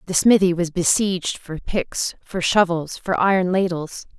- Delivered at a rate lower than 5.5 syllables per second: Yes, 4.5 syllables/s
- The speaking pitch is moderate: Yes, medium, 180 Hz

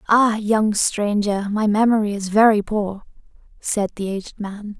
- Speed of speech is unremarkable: Yes, average, 150 wpm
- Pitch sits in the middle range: No, high, 210 Hz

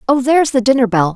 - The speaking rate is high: Yes, fast, 260 wpm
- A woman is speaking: Yes, female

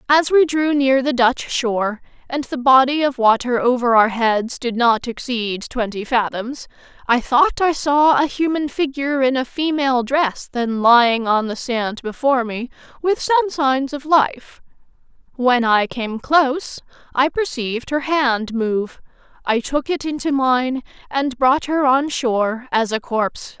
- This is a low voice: No, very high, 255 Hz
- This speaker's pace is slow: No, average, 165 wpm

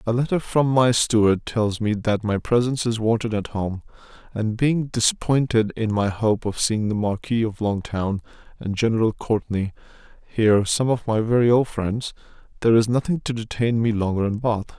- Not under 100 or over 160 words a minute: No, average, 185 wpm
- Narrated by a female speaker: No, male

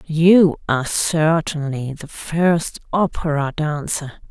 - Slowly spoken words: Yes, slow, 100 wpm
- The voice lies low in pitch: No, medium, 155 Hz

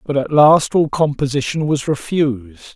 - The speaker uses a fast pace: No, average, 155 wpm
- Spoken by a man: Yes, male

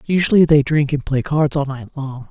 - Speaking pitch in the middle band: Yes, medium, 145 Hz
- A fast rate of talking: Yes, fast, 235 wpm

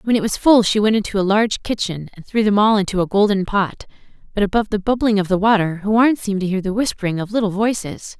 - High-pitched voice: Yes, high, 205 Hz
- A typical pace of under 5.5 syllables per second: No, 6.4 syllables/s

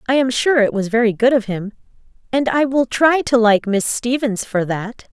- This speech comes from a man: No, female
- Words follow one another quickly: Yes, fast, 220 wpm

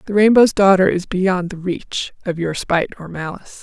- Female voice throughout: Yes, female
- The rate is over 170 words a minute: Yes, average, 200 wpm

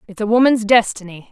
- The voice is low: No, high, 215 Hz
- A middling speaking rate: Yes, average, 185 wpm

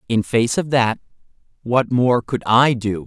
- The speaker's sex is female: No, male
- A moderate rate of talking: Yes, average, 175 wpm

